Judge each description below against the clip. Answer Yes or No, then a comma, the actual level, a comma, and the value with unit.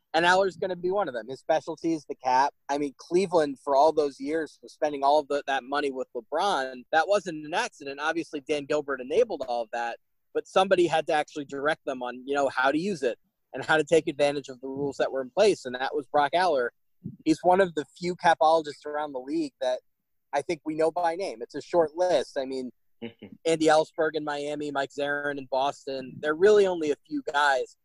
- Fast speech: Yes, fast, 230 wpm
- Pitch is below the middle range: No, medium, 150 Hz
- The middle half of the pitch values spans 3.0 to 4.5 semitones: Yes, average, 3.9 semitones